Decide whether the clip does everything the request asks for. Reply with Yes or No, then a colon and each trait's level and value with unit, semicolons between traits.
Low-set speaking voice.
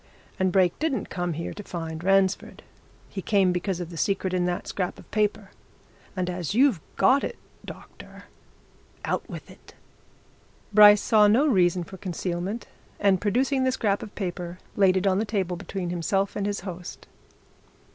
No: high, 190 Hz